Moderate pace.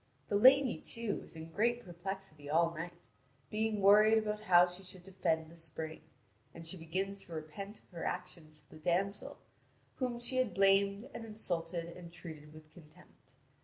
Yes: average, 170 wpm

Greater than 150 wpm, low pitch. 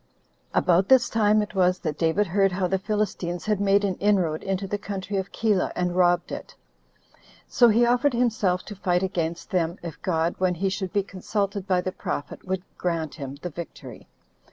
No: average, 195 wpm; high, 190 Hz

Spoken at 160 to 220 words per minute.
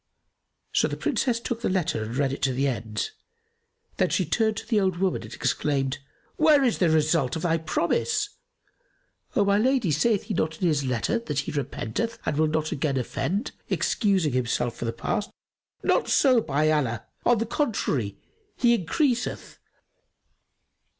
Yes: average, 170 wpm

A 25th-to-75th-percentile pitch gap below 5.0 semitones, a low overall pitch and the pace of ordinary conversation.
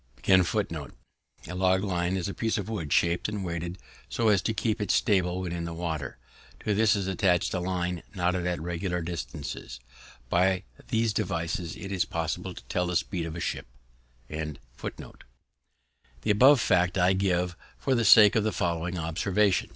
Yes: average, 2.8 semitones; very low, 90 Hz; average, 160 wpm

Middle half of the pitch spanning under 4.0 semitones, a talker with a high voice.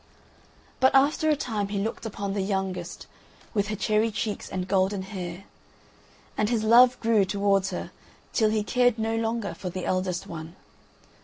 Yes: average, 2.9 semitones; high, 205 Hz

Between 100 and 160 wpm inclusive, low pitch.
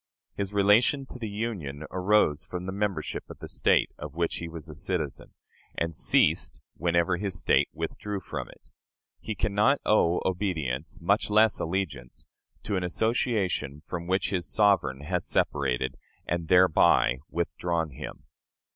Yes: average, 150 wpm; very low, 90 Hz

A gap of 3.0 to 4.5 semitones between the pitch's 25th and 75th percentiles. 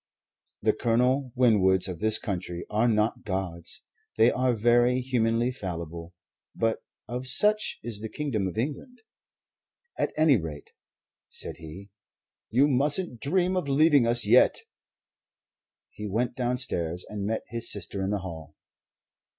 No: average, 5.1 semitones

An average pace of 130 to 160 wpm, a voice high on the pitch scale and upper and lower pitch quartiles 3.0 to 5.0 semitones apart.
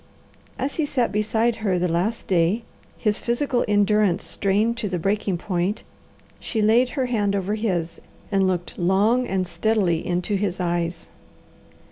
Yes: average, 150 wpm; high, 205 Hz; average, 3.7 semitones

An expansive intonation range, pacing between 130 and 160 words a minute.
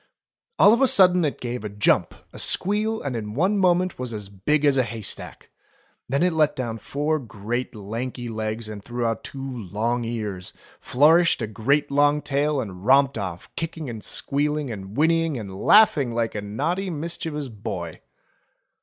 No: wide, 5.8 semitones; average, 170 wpm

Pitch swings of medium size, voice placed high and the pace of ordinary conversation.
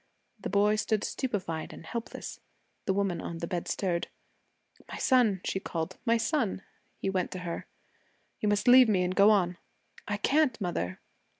Yes: average, 3.7 semitones; high, 200 Hz; average, 170 wpm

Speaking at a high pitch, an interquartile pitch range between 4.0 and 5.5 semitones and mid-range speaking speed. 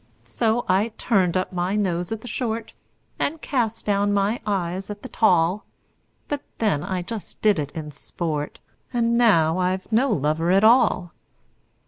Yes: high, 200 Hz; average, 4.4 semitones; average, 160 wpm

